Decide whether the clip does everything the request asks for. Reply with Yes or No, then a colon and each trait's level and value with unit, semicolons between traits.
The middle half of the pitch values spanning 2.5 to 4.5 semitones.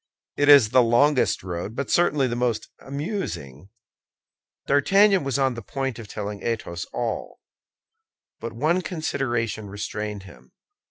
No: average, 5.3 semitones